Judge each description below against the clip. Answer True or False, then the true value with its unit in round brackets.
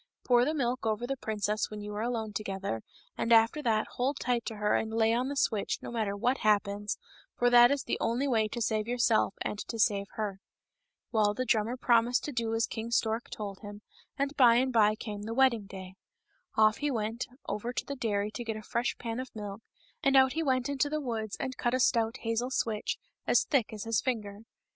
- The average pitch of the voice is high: True (225 Hz)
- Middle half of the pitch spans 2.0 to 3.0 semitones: True (2.7 semitones)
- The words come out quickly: True (220 wpm)